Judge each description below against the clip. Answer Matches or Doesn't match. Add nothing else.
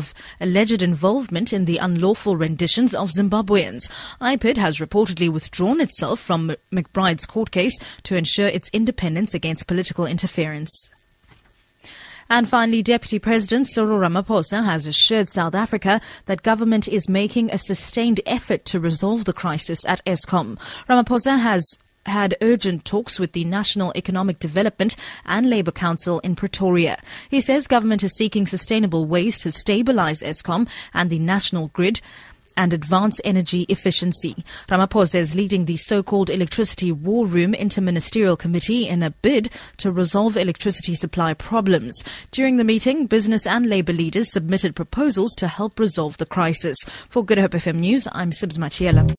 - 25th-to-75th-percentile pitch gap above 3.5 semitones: Matches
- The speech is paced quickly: Doesn't match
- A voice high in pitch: Matches